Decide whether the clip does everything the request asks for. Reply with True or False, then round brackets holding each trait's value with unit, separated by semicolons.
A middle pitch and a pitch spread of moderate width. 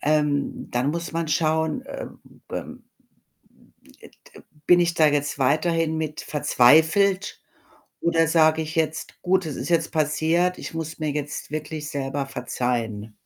False (155 Hz; 2.2 semitones)